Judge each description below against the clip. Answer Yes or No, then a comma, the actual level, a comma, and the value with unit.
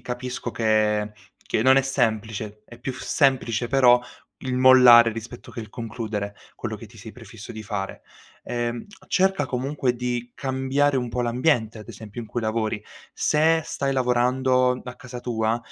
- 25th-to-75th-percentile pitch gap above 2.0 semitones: Yes, average, 2.7 semitones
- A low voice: Yes, low, 120 Hz